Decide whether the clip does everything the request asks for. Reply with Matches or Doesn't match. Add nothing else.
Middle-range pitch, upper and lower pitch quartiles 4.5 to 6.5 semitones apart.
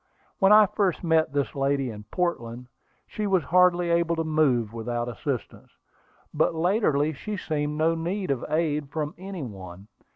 Matches